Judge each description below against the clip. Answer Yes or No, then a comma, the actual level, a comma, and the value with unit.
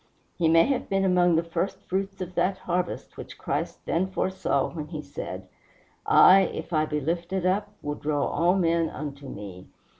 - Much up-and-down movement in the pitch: No, average, 3.6 semitones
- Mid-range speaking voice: Yes, medium, 170 Hz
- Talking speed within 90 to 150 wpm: No, average, 180 wpm